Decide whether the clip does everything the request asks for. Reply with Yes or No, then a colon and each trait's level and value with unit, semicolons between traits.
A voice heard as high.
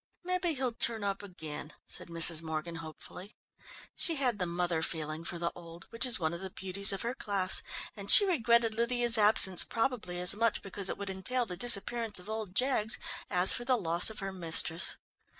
Yes: high, 200 Hz